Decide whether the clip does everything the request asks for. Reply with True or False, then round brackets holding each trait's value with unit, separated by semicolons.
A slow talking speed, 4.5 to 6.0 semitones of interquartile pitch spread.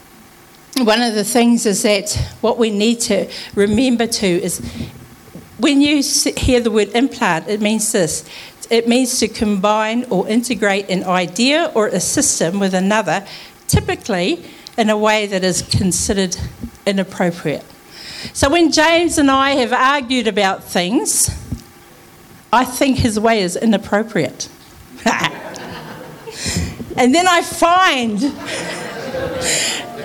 True (125 wpm; 4.9 semitones)